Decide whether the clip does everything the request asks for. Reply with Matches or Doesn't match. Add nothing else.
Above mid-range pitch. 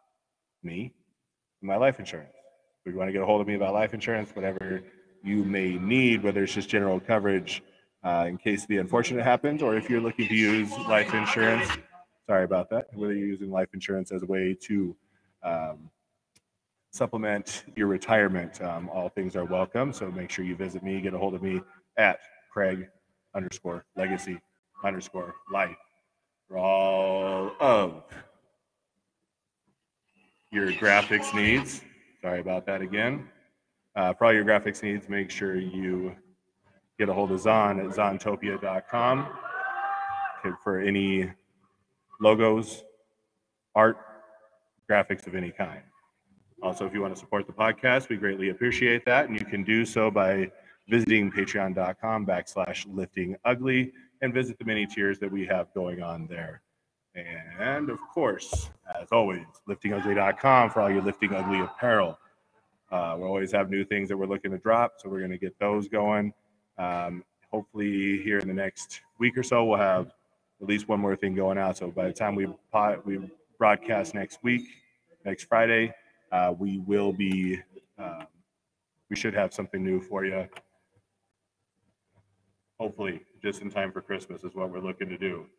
Doesn't match